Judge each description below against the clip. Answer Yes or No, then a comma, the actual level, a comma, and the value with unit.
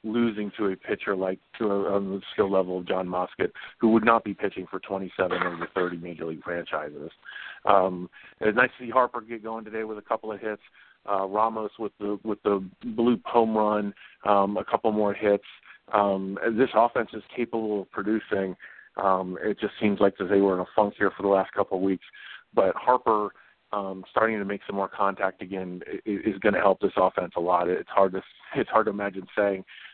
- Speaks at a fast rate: Yes, fast, 210 wpm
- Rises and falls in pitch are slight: Yes, narrow, 2.2 semitones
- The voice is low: Yes, low, 100 Hz